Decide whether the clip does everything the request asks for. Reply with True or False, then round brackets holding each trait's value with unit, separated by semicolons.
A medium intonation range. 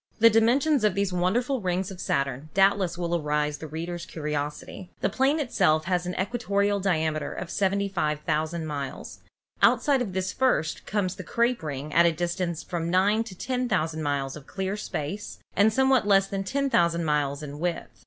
True (4.7 semitones)